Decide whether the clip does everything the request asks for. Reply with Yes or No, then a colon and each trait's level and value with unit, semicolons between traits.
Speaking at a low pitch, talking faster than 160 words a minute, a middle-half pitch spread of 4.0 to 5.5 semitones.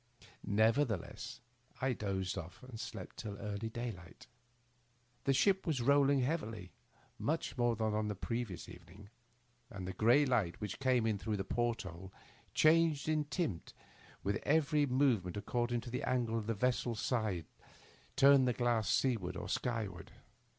No: low, 115 Hz; average, 155 wpm; average, 4.3 semitones